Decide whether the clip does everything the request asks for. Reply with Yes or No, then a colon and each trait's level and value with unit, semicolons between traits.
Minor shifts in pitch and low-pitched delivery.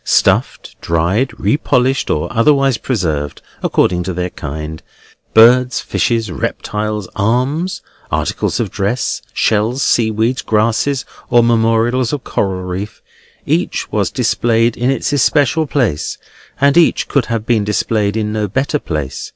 No: average, 4.2 semitones; low, 115 Hz